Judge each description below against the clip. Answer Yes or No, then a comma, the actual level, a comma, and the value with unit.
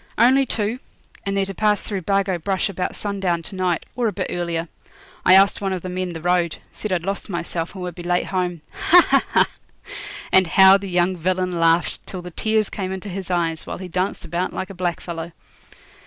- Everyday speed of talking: No, fast, 215 wpm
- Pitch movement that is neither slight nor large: No, narrow, 2.2 semitones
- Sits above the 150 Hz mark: Yes, medium, 185 Hz